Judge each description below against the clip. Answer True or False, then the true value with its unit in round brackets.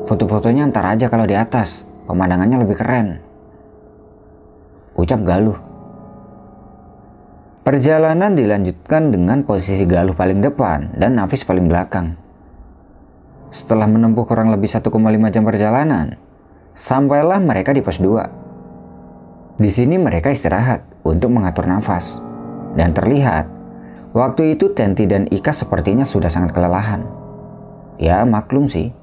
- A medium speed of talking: True (115 wpm)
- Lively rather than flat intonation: True (6.0 semitones)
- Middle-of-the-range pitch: False (110 Hz)